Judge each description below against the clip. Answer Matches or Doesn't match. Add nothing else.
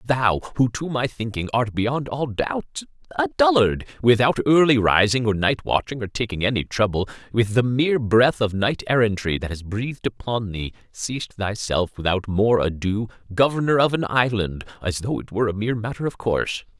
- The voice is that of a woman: Doesn't match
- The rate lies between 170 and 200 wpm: Matches